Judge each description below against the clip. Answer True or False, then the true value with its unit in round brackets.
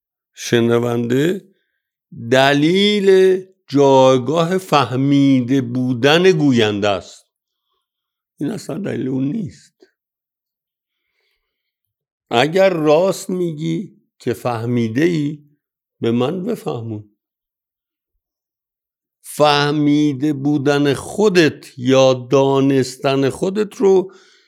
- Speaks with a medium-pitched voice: True (145 Hz)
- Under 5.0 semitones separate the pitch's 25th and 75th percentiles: False (5.4 semitones)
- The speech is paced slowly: True (70 wpm)